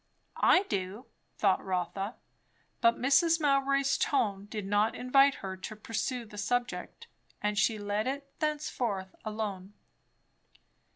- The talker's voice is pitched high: Yes, high, 220 Hz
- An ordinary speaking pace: No, slow, 120 wpm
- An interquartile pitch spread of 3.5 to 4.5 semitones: No, average, 5.2 semitones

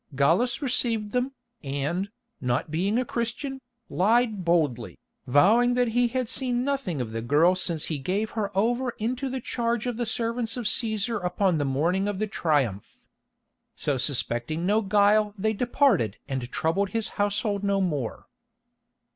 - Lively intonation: Yes, wide, 6.7 semitones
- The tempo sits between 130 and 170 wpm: Yes, average, 155 wpm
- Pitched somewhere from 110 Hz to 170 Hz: No, high, 205 Hz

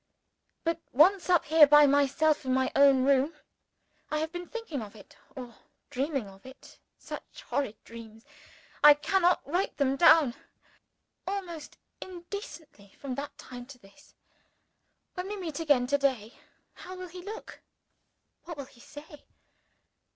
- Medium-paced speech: Yes, average, 145 wpm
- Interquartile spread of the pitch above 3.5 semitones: Yes, average, 4.7 semitones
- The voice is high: Yes, very high, 290 Hz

